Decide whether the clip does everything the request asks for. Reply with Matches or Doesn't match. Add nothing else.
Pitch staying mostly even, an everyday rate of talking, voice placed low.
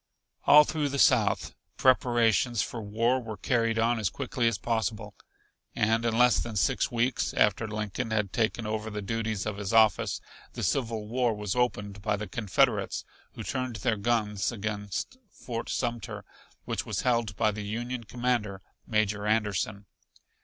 Matches